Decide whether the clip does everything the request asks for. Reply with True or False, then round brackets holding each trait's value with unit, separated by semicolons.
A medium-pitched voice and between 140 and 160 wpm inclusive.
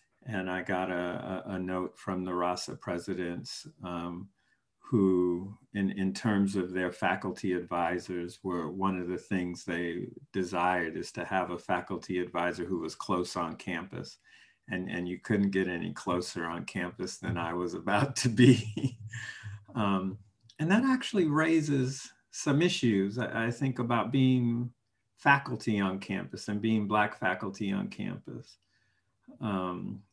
False (95 Hz; 145 wpm)